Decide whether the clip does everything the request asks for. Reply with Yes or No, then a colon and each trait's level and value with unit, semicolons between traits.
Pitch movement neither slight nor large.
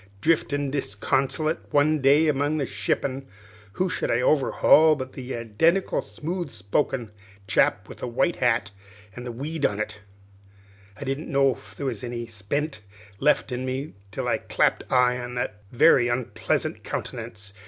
Yes: average, 3.8 semitones